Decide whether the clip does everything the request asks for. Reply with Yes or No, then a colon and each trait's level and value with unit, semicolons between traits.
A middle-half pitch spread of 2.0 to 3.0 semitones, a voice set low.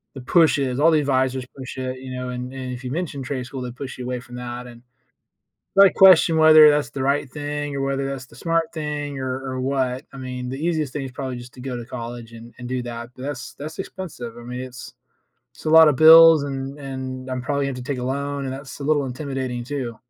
Yes: narrow, 2.5 semitones; low, 130 Hz